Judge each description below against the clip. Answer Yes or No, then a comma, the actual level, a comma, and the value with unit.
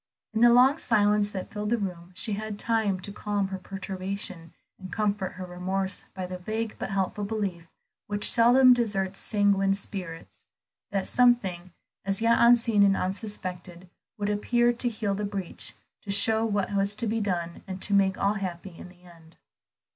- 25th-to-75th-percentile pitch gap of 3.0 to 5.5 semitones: No, narrow, 2.6 semitones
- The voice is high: Yes, high, 200 Hz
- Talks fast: No, average, 175 wpm